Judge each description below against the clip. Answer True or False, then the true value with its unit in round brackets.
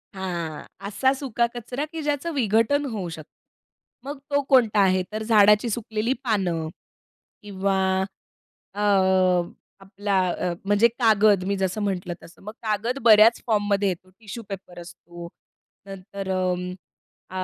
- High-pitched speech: True (205 Hz)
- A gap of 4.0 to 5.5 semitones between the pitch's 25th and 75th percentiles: False (3.4 semitones)